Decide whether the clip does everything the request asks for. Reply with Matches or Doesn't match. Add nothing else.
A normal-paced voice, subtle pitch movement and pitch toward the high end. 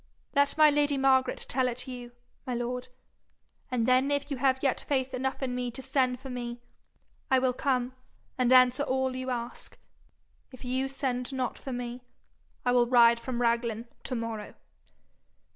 Matches